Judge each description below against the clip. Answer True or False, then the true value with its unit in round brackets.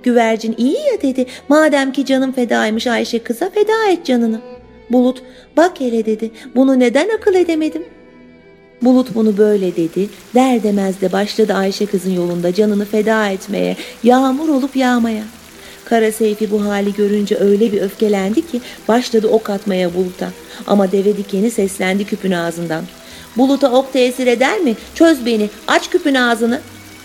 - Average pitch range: True (4.2 semitones)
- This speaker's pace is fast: True (150 wpm)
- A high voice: True (225 Hz)